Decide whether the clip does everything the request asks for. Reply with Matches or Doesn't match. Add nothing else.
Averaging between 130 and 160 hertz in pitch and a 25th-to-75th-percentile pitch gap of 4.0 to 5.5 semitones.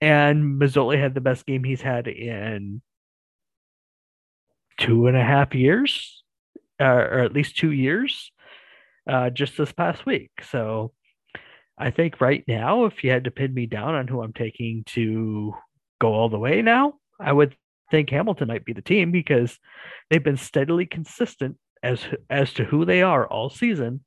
Matches